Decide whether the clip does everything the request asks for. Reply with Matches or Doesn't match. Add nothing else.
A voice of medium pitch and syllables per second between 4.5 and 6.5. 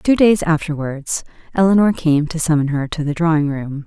Matches